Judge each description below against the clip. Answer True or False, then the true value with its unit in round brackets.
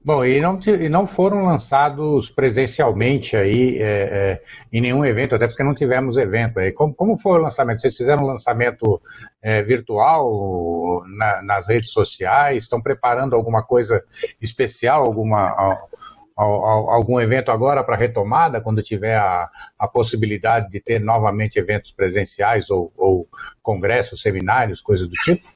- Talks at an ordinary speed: True (155 wpm)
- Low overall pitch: True (120 Hz)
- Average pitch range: True (4.7 semitones)